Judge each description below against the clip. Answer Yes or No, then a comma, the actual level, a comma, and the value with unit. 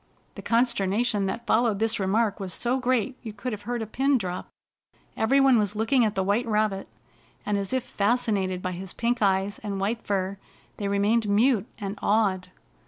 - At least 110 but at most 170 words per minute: No, average, 185 wpm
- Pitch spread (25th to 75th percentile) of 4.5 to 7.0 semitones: No, average, 3.1 semitones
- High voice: Yes, high, 210 Hz